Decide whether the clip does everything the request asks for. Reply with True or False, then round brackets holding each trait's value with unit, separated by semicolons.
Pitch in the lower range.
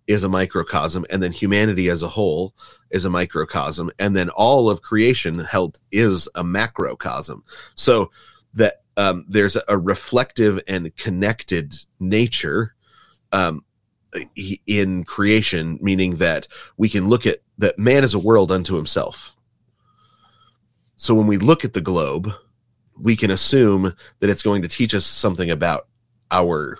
True (100 Hz)